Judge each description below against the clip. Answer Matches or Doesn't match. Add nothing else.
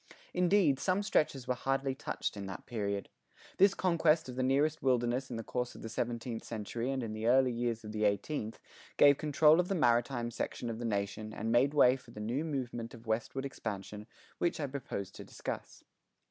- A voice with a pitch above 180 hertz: Doesn't match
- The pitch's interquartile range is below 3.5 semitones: Doesn't match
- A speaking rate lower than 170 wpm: Doesn't match